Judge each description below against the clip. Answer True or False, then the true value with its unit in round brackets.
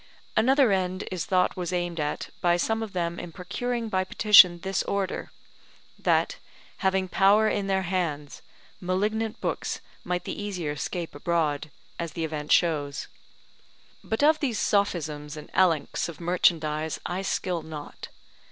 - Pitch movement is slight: False (3.6 semitones)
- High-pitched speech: False (180 Hz)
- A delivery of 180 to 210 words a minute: False (145 wpm)